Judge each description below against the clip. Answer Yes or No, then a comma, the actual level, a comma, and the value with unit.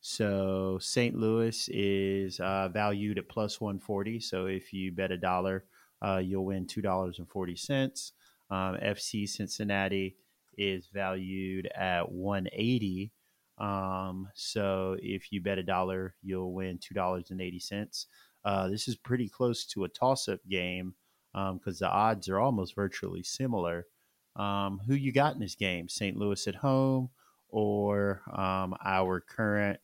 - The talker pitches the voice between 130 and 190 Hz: No, very low, 95 Hz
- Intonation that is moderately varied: No, narrow, 1.8 semitones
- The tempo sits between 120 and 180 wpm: Yes, average, 140 wpm